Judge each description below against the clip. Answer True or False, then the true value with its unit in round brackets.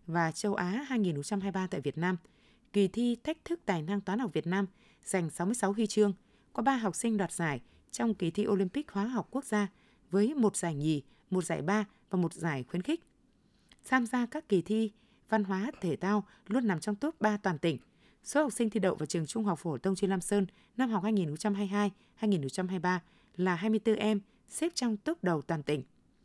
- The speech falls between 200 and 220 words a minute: True (205 wpm)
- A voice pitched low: False (205 Hz)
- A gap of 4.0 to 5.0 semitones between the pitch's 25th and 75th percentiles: False (3.5 semitones)